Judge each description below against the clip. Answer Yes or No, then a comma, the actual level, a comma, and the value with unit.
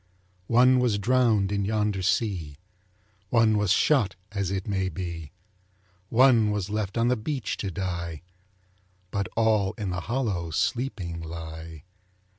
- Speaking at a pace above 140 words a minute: No, slow, 135 wpm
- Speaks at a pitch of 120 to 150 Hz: No, low, 100 Hz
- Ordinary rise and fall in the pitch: Yes, average, 4.2 semitones